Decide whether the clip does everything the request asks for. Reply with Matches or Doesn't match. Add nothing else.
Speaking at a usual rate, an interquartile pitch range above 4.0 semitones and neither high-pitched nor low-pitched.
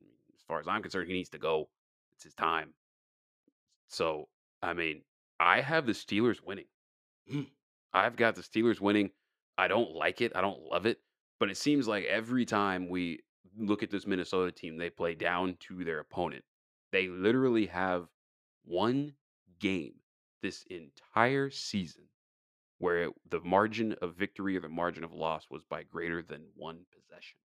Doesn't match